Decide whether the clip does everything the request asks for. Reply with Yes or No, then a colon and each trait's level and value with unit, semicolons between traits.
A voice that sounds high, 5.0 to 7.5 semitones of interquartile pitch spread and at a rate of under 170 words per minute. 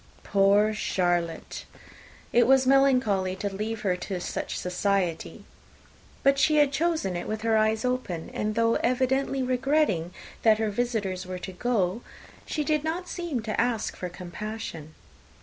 Yes: high, 220 Hz; wide, 5.6 semitones; average, 150 wpm